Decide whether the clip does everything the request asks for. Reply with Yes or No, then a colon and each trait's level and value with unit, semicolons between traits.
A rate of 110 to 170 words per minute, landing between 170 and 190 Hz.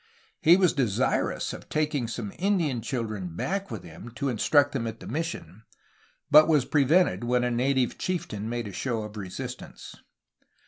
No: average, 150 wpm; low, 125 Hz